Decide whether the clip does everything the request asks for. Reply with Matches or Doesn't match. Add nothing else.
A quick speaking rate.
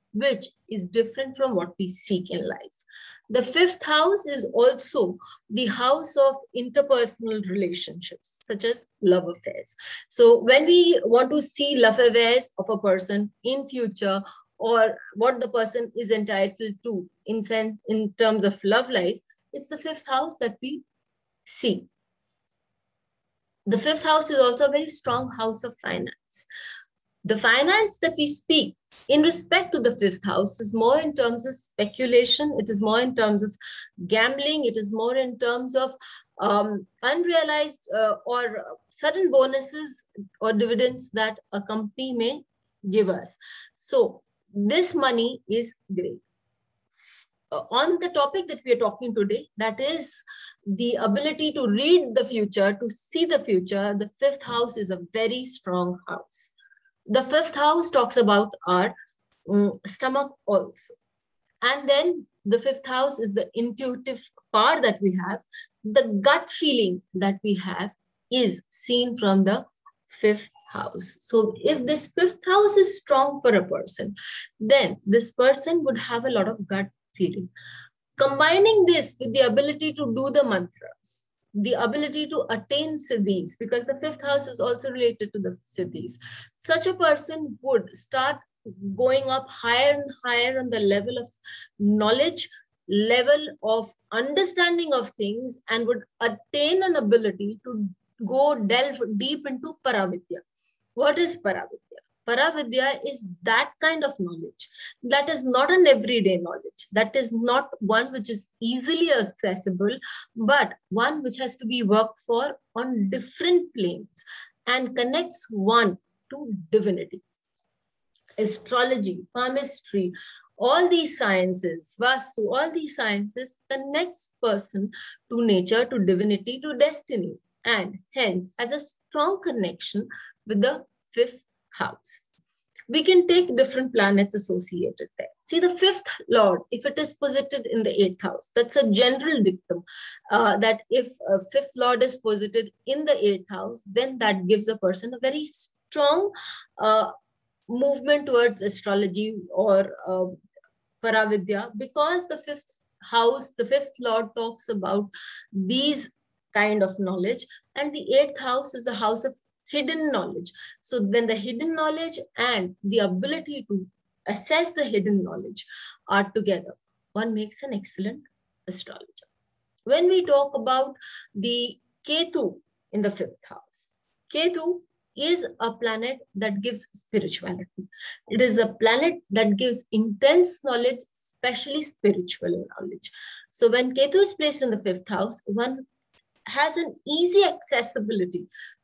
Doesn't match